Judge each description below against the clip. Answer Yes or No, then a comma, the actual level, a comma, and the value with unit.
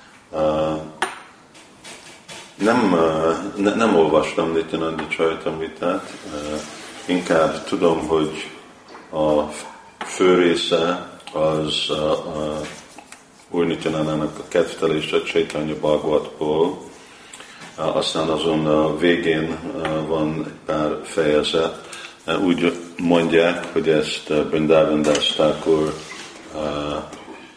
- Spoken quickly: No, slow, 105 wpm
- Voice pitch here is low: Yes, very low, 80 Hz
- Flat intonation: Yes, narrow, 1.2 semitones